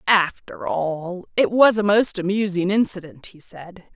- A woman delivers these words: Yes, female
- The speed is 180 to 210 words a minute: No, average, 150 wpm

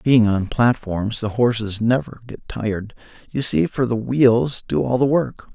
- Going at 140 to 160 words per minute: No, average, 185 wpm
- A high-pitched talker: No, low, 115 Hz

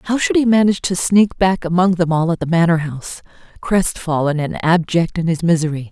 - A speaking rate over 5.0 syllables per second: Yes, 5.5 syllables/s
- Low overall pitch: No, medium, 170 Hz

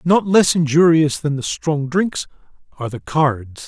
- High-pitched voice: No, medium, 155 Hz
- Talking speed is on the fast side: No, average, 165 wpm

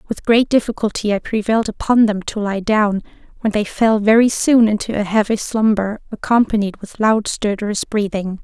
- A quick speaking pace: No, average, 170 wpm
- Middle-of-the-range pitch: No, high, 215 Hz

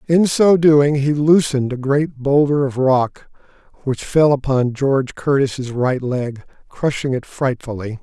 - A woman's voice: No, male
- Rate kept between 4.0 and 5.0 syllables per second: Yes, 4.1 syllables/s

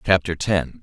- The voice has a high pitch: No, very low, 85 Hz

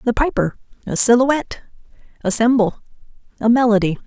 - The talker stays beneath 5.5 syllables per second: No, 5.8 syllables/s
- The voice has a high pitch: Yes, high, 230 Hz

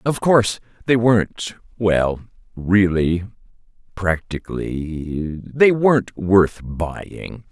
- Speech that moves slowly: Yes, slow, 90 wpm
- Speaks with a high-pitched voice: No, low, 100 Hz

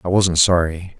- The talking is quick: No, average, 180 wpm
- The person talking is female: No, male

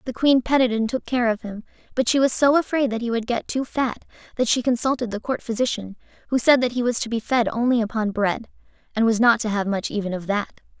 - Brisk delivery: Yes, fast, 250 wpm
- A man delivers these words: No, female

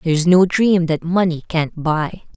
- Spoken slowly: No, fast, 205 wpm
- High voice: No, medium, 170 Hz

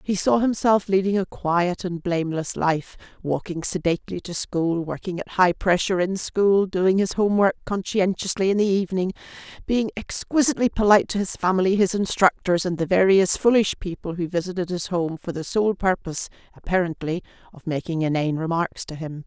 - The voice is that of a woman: Yes, female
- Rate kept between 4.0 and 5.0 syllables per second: No, 5.5 syllables/s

